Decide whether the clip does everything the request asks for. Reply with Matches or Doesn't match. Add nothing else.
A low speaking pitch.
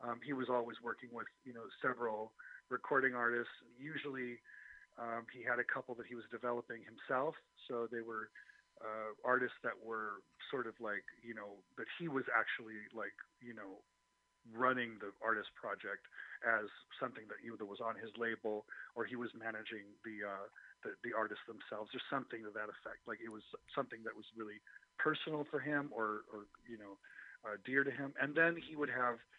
Matches